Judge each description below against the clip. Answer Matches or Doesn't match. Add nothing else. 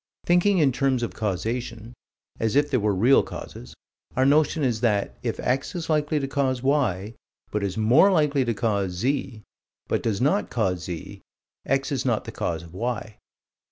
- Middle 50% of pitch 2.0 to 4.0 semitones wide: Doesn't match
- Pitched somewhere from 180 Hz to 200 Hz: Doesn't match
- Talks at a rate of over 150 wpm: Matches